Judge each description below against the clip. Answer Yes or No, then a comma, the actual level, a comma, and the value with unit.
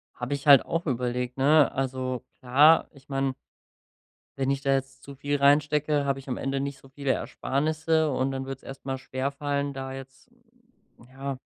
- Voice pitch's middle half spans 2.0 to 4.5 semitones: No, narrow, 1.3 semitones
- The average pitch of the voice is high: No, low, 135 Hz